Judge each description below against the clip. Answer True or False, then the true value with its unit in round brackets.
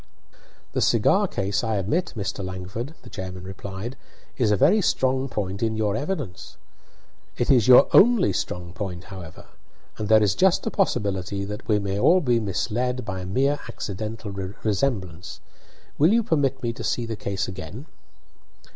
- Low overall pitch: True (105 Hz)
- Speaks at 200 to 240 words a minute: False (165 wpm)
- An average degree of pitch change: True (5.0 semitones)